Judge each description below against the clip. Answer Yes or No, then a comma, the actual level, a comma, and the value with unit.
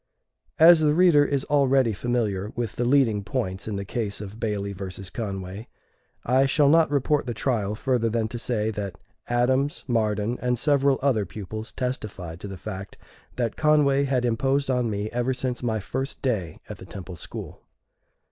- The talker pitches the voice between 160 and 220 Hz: No, low, 120 Hz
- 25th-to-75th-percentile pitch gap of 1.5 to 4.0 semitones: No, average, 4.6 semitones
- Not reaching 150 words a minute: No, average, 175 wpm